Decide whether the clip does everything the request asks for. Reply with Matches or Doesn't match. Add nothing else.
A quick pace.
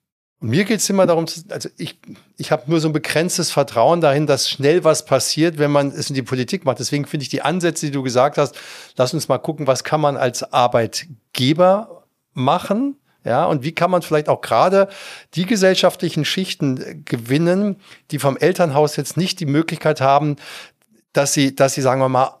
Matches